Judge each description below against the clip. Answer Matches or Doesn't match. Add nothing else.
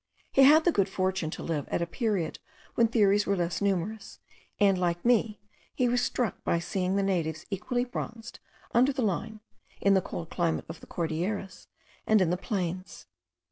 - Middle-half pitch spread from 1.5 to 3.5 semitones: Doesn't match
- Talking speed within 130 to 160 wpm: Doesn't match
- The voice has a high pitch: Matches